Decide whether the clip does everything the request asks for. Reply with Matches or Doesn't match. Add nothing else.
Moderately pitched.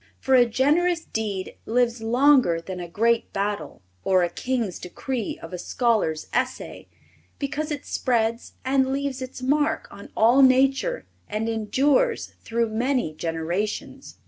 Doesn't match